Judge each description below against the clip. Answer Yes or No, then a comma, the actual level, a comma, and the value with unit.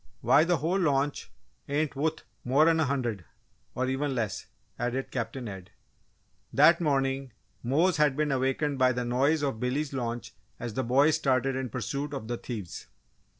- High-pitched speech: No, low, 135 Hz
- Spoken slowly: No, average, 160 wpm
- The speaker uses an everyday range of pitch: Yes, average, 3.2 semitones